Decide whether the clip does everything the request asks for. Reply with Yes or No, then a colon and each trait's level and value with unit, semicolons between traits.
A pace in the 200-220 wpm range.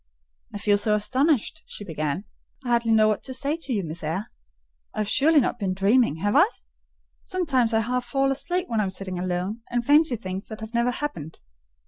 Yes: fast, 205 wpm